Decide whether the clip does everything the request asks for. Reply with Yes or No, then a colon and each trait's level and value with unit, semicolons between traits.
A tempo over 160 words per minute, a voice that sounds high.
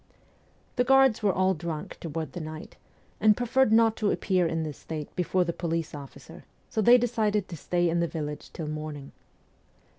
No: average, 175 wpm; medium, 175 Hz